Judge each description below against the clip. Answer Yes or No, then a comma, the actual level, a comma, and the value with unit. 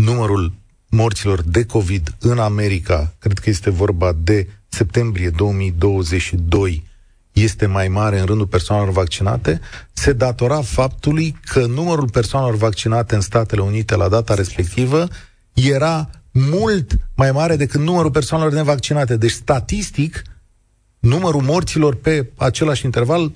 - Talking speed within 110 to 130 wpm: Yes, average, 125 wpm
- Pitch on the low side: Yes, low, 115 Hz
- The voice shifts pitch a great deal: Yes, wide, 6.0 semitones